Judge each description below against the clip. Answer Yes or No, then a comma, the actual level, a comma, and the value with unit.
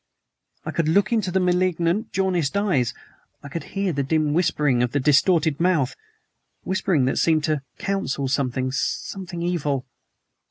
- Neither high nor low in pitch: Yes, medium, 165 Hz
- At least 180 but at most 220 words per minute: No, average, 150 wpm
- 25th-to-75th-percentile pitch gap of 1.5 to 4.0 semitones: No, average, 4.8 semitones